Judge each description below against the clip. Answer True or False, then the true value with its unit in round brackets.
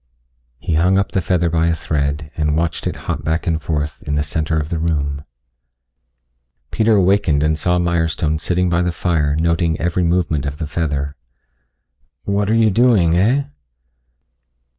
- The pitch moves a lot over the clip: False (2.7 semitones)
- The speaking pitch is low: True (80 Hz)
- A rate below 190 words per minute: True (165 wpm)